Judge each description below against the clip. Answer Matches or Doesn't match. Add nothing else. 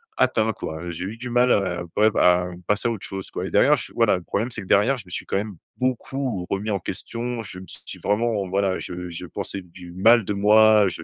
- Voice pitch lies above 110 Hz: Doesn't match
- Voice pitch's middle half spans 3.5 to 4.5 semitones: Matches